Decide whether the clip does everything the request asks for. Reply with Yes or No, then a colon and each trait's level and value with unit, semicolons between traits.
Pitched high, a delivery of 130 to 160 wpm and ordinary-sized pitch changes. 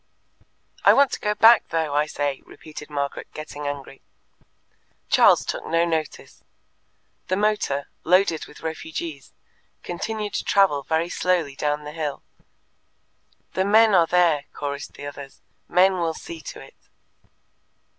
No: medium, 160 Hz; slow, 135 wpm; average, 4.0 semitones